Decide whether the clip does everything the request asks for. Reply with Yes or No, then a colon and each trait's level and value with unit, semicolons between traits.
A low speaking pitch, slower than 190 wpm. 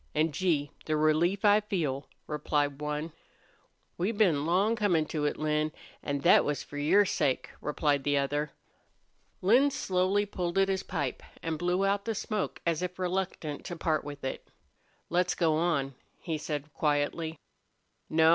No: medium, 160 Hz; average, 160 wpm